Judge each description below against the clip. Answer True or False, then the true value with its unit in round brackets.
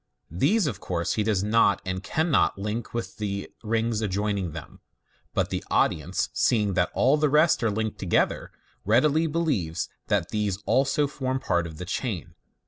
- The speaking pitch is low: True (105 Hz)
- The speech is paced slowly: False (165 wpm)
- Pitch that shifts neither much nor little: False (6.1 semitones)